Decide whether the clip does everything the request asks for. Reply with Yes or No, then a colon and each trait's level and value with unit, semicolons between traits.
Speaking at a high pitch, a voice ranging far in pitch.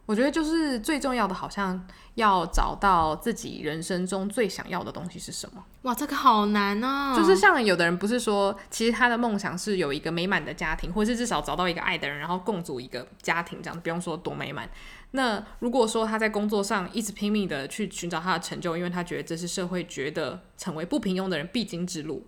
No: high, 195 Hz; average, 4.6 semitones